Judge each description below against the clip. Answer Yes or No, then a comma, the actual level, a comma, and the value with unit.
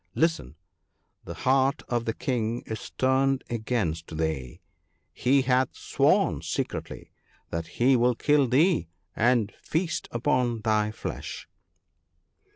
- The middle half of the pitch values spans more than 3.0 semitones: Yes, average, 3.6 semitones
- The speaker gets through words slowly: Yes, slow, 120 wpm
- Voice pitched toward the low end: Yes, low, 120 Hz